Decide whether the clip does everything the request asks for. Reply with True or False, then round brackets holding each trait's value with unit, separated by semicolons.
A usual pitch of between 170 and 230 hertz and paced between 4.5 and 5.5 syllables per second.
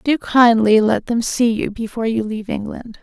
True (225 Hz; 5.1 syllables/s)